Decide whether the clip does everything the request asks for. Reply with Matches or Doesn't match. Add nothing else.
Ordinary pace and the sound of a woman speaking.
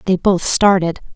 Matches